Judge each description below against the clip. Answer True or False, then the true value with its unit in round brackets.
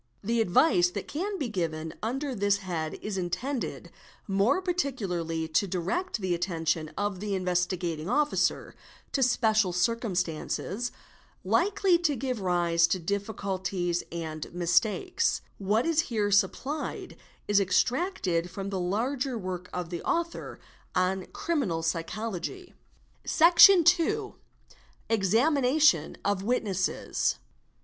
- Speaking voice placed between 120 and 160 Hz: False (200 Hz)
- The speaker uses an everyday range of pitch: False (6.9 semitones)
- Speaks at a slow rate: True (120 wpm)